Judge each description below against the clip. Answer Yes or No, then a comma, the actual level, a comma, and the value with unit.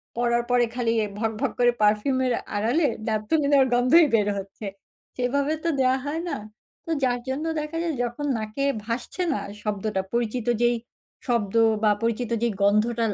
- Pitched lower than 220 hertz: No, high, 240 Hz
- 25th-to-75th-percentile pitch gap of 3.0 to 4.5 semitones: Yes, average, 4.0 semitones